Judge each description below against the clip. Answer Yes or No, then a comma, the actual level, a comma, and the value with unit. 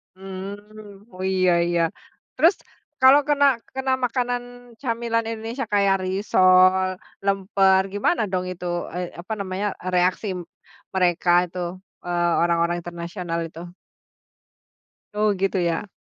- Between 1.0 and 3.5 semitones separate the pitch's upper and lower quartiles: Yes, average, 3.2 semitones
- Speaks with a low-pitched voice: No, high, 190 Hz